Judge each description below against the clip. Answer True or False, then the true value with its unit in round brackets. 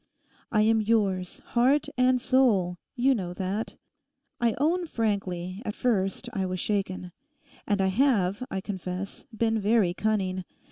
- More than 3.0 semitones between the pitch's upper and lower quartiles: True (4.0 semitones)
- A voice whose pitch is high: True (205 Hz)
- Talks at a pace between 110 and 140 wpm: True (135 wpm)